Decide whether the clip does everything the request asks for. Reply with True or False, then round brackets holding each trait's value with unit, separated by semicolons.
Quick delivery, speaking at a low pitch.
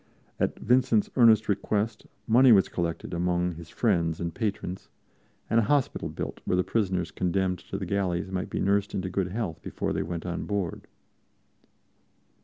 False (165 wpm; 95 Hz)